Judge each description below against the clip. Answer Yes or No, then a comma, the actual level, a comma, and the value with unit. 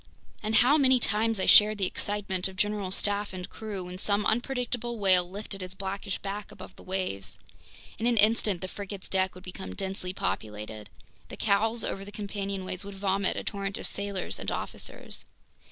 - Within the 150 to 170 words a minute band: No, average, 180 wpm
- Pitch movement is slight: Yes, narrow, 2.1 semitones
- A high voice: Yes, high, 200 Hz